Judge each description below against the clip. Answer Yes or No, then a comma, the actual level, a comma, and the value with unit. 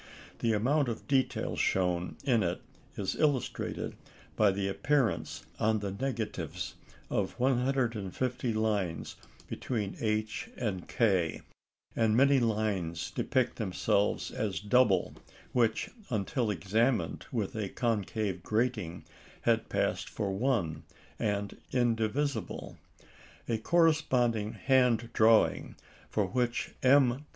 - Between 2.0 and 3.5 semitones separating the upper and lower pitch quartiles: No, average, 3.9 semitones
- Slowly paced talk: Yes, slow, 105 wpm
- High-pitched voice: No, low, 110 Hz